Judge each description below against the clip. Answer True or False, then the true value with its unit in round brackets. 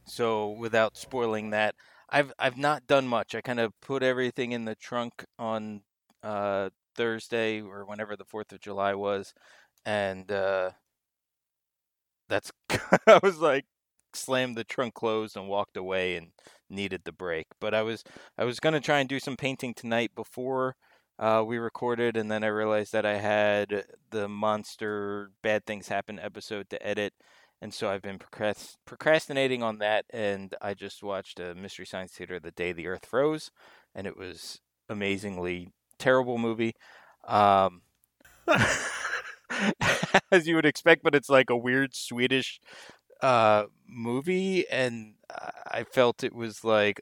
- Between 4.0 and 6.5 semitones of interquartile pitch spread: False (3.6 semitones)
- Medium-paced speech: True (155 wpm)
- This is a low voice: True (110 Hz)